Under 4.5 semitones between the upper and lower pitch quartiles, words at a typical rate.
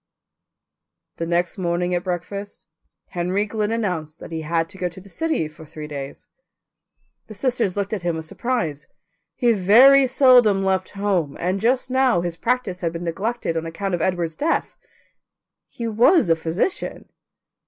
No: wide, 5.4 semitones; average, 165 wpm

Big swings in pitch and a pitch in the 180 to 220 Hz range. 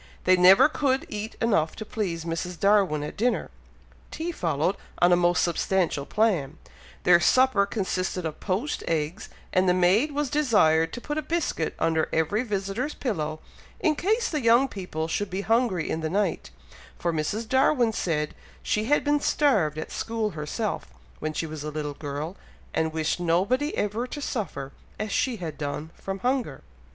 Yes: wide, 6.7 semitones; high, 190 Hz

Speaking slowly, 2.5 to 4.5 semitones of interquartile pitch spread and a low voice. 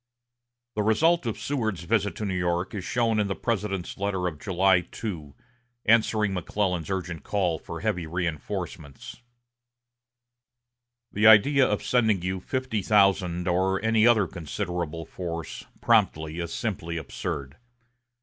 Yes: slow, 130 wpm; average, 3.7 semitones; very low, 95 Hz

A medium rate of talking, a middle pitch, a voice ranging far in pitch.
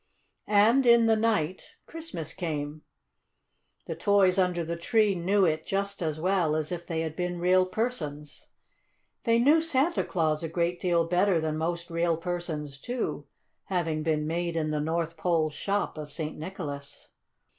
No: average, 160 wpm; medium, 170 Hz; average, 3.8 semitones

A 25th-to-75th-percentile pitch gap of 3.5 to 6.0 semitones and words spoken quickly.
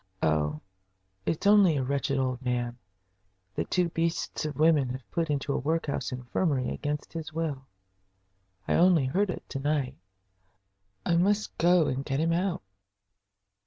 No: average, 4.2 semitones; average, 150 wpm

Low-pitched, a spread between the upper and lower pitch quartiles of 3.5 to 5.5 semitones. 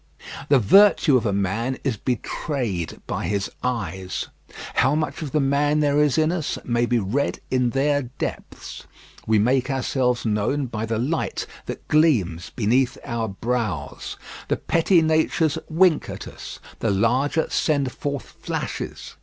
Yes: low, 130 Hz; average, 4.7 semitones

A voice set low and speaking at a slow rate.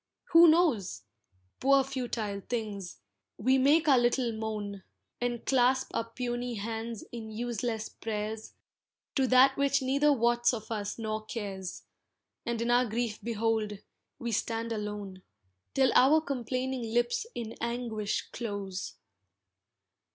No: high, 235 Hz; slow, 125 wpm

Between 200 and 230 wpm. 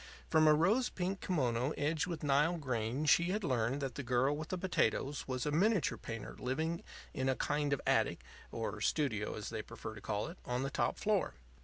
Yes: fast, 205 wpm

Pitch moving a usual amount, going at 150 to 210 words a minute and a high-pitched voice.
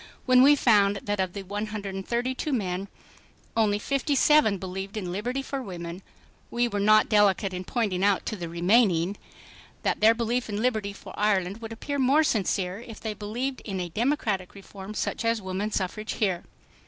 Yes: average, 3.6 semitones; average, 180 wpm; high, 210 Hz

